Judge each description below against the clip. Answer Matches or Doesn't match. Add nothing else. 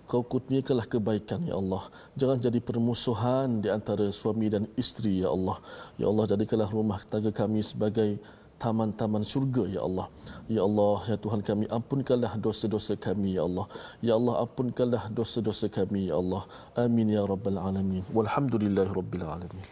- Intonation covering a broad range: Doesn't match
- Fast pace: Matches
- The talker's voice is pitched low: Matches